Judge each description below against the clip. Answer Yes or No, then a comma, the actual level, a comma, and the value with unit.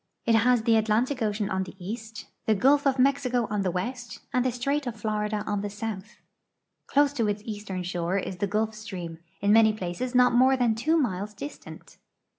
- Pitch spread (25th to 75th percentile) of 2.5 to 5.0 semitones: Yes, average, 3.5 semitones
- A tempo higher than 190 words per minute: Yes, average, 200 wpm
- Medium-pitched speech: No, high, 220 Hz